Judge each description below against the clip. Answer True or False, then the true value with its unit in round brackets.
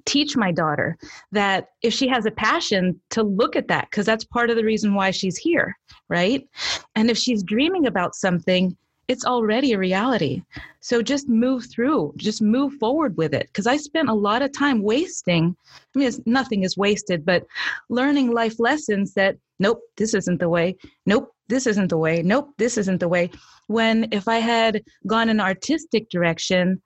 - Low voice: False (220 Hz)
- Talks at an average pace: True (190 wpm)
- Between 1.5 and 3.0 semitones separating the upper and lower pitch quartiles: False (4.7 semitones)